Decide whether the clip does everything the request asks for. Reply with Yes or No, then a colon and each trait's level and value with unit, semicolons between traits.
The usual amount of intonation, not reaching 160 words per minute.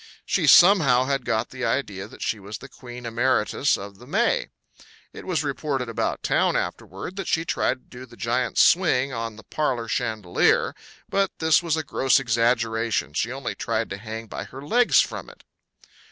No: average, 4.2 semitones; average, 180 wpm